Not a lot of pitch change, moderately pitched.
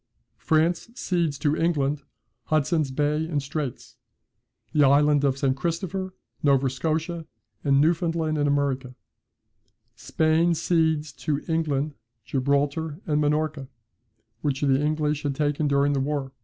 Yes: narrow, 2.2 semitones; medium, 150 Hz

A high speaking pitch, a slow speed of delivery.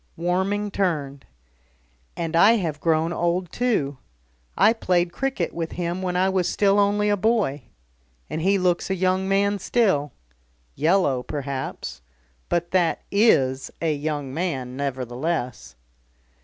No: medium, 175 Hz; slow, 130 wpm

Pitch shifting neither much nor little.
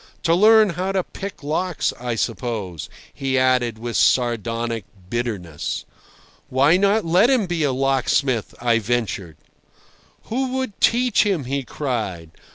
No: wide, 7.9 semitones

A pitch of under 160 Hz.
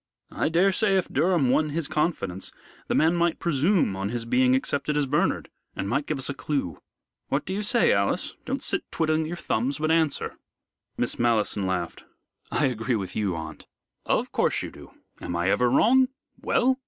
Yes: medium, 140 Hz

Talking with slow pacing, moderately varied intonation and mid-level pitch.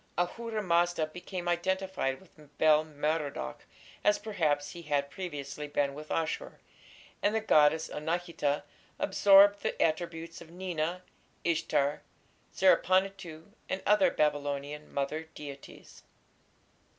Yes: slow, 110 wpm; average, 3.8 semitones; medium, 165 Hz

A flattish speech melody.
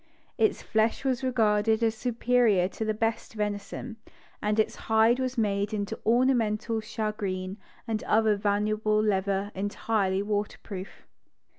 Yes: narrow, 1.7 semitones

